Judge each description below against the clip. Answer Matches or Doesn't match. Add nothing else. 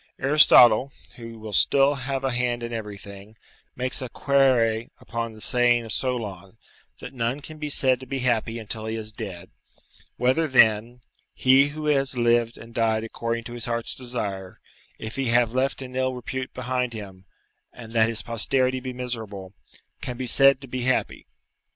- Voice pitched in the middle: Doesn't match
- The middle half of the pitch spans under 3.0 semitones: Matches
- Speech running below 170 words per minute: Doesn't match